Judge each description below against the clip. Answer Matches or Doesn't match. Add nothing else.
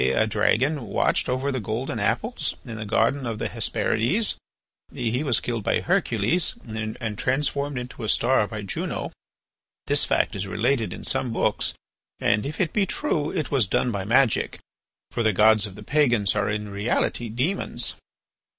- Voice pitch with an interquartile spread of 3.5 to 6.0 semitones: Matches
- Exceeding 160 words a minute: Matches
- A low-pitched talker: Matches